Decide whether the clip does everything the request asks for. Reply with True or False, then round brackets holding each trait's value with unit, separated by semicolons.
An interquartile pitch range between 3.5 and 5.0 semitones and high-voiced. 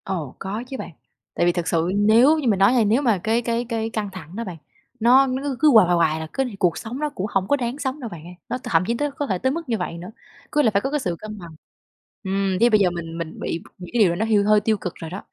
False (5.5 semitones; 215 Hz)